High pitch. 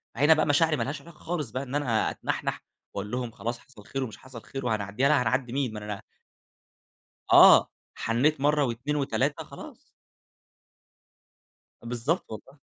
No: low, 130 Hz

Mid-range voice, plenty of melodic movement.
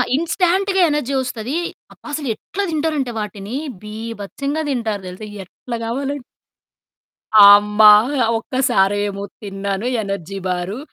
No: high, 225 Hz; wide, 5.7 semitones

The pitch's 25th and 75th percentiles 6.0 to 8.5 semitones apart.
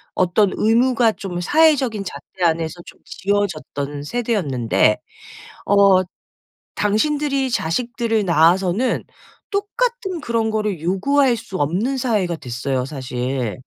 Yes: wide, 7.0 semitones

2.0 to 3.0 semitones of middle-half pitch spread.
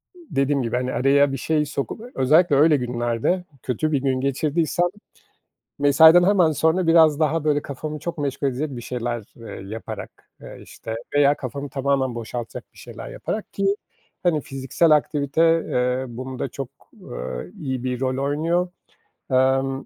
No: average, 3.5 semitones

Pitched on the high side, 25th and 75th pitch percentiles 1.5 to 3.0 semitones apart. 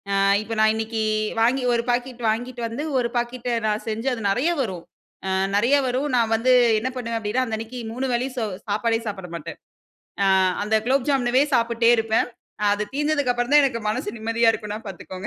Yes: high, 235 Hz; narrow, 2.4 semitones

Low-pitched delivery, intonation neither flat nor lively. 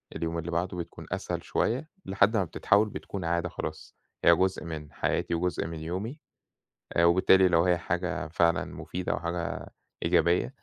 No: very low, 85 Hz; narrow, 2.0 semitones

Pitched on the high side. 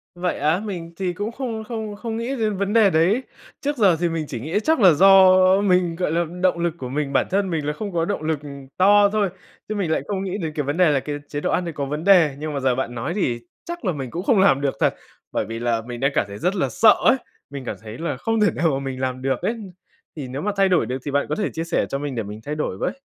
No: medium, 170 Hz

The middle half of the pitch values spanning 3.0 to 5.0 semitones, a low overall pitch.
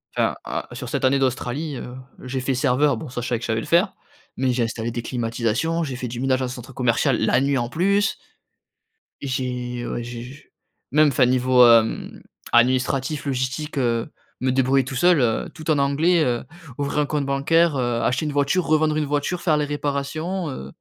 Yes: average, 3.4 semitones; low, 130 Hz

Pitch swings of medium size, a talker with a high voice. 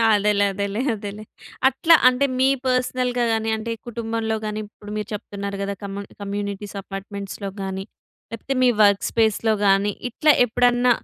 Yes: average, 3.2 semitones; high, 210 Hz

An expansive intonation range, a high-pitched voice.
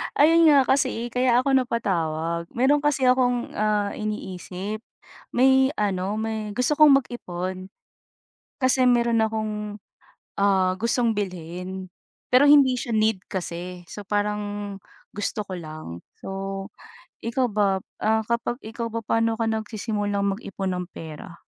No: average, 4.0 semitones; high, 215 Hz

